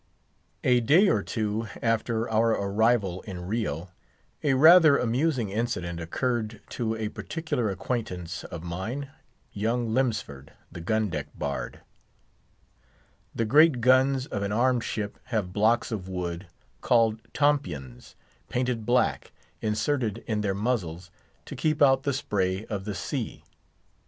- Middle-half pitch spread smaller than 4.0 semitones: No, average, 4.7 semitones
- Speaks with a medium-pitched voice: No, low, 110 Hz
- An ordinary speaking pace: No, slow, 130 wpm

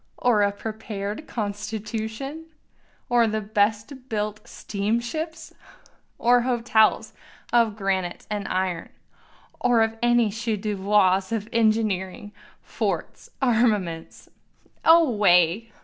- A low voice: No, high, 215 Hz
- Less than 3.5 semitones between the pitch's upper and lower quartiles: Yes, narrow, 2.6 semitones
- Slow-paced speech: Yes, slow, 90 wpm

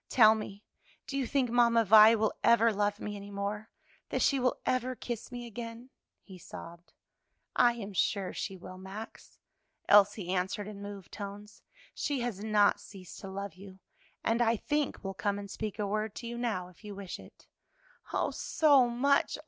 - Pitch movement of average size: Yes, average, 3.0 semitones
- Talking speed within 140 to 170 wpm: No, average, 180 wpm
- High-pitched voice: Yes, high, 210 Hz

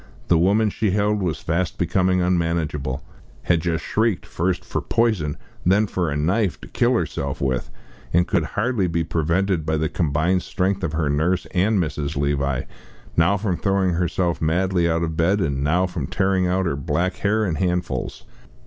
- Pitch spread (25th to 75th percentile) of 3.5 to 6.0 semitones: No, average, 3.1 semitones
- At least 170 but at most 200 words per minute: Yes, average, 175 wpm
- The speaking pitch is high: No, very low, 85 Hz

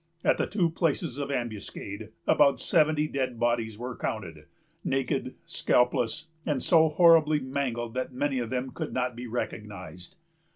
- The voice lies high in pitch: No, low, 130 Hz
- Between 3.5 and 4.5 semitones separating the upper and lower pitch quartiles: Yes, average, 4.1 semitones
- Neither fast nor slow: Yes, average, 150 wpm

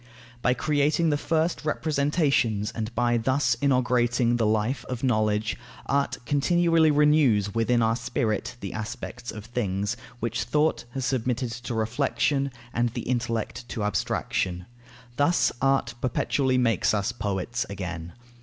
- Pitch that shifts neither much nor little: Yes, average, 4.1 semitones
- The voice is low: Yes, low, 120 Hz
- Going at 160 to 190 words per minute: No, slow, 135 wpm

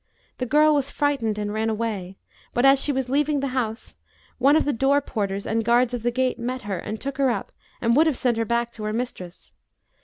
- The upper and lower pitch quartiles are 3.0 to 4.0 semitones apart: Yes, average, 3.7 semitones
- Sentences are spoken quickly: Yes, fast, 235 wpm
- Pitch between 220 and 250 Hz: Yes, high, 245 Hz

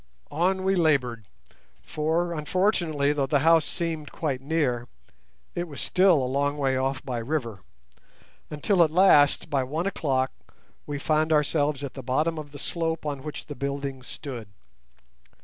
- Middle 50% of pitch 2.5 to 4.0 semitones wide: Yes, average, 3.2 semitones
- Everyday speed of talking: Yes, average, 155 wpm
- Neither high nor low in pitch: Yes, medium, 145 Hz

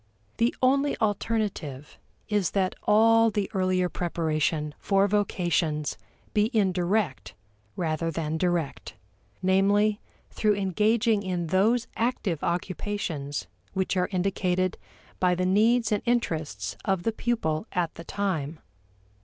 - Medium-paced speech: No, slow, 115 wpm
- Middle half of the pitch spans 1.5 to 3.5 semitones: No, average, 4.1 semitones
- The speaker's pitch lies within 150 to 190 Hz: Yes, medium, 185 Hz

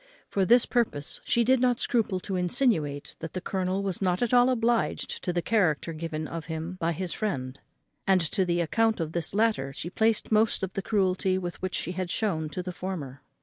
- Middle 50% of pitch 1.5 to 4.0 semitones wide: No, average, 4.6 semitones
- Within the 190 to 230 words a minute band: Yes, fast, 205 wpm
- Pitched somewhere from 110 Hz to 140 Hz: No, medium, 185 Hz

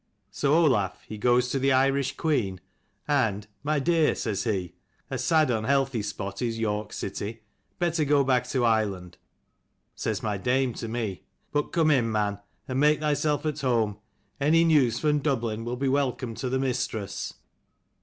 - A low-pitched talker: Yes, low, 125 Hz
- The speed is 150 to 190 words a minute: Yes, average, 165 wpm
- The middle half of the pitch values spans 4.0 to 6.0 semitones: Yes, average, 4.8 semitones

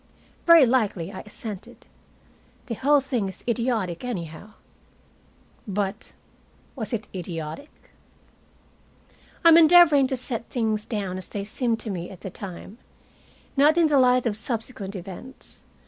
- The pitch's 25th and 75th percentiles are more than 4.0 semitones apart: Yes, average, 5.1 semitones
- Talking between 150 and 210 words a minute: No, slow, 135 wpm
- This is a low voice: No, high, 225 Hz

